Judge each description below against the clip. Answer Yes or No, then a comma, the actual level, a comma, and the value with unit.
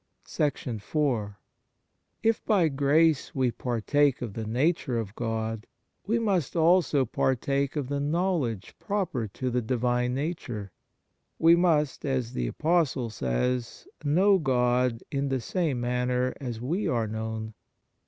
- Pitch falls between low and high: No, low, 130 Hz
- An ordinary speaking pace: No, slow, 130 wpm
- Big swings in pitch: No, average, 4.9 semitones